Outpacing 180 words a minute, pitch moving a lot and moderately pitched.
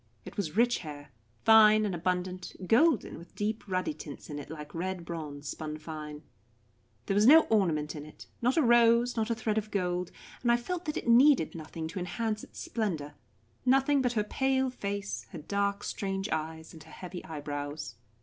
No: average, 190 wpm; wide, 6.5 semitones; high, 195 Hz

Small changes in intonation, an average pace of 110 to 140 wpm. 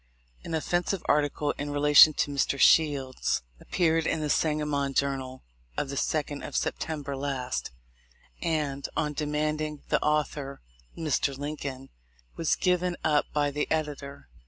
Yes: narrow, 1.7 semitones; slow, 135 wpm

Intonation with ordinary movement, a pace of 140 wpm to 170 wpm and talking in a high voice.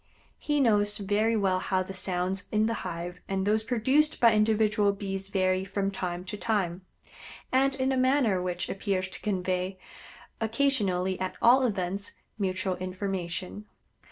Yes: average, 3.0 semitones; average, 150 wpm; high, 195 Hz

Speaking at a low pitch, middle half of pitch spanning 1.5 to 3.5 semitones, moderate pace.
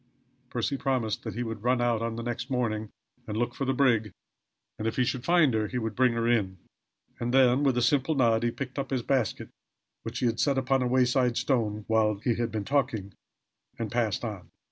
No: low, 120 Hz; narrow, 2.6 semitones; fast, 220 wpm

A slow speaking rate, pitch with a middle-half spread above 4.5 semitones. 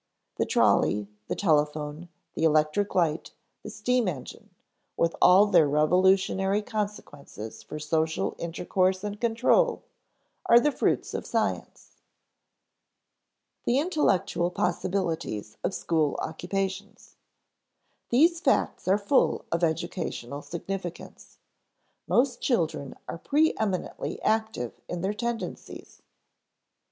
Yes: slow, 105 wpm; average, 5.0 semitones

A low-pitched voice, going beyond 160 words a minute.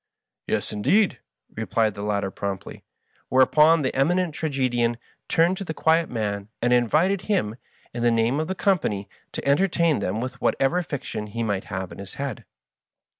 Yes: low, 125 Hz; average, 170 wpm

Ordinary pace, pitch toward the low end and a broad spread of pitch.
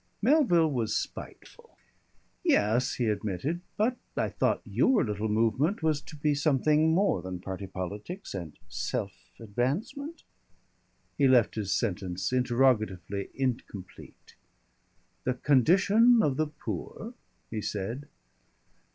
No: slow, 115 wpm; low, 125 Hz; wide, 7.4 semitones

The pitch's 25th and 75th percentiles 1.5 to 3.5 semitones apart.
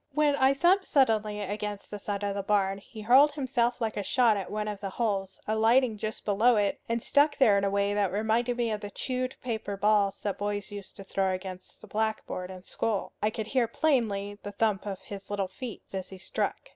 Yes: average, 3.0 semitones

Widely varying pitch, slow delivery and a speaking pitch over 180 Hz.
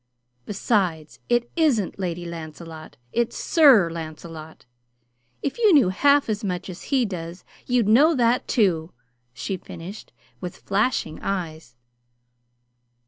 Yes: wide, 6.4 semitones; slow, 120 wpm; high, 190 Hz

